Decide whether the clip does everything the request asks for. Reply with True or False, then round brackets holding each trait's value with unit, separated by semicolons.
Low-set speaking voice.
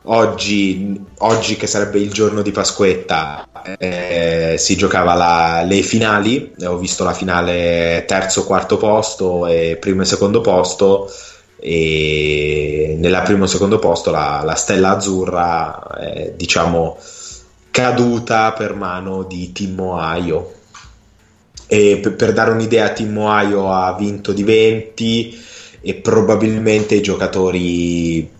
True (95 Hz)